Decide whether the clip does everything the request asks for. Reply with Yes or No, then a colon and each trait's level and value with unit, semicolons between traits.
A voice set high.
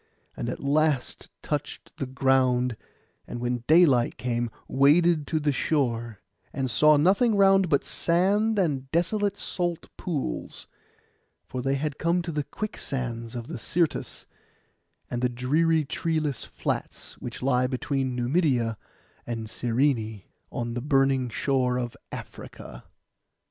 No: low, 135 Hz